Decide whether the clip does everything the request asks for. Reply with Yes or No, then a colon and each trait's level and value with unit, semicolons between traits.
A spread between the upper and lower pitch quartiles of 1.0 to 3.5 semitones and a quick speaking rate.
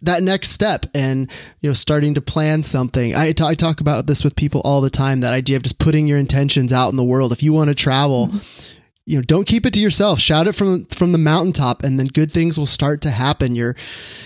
Yes: average, 3.0 semitones; fast, 240 wpm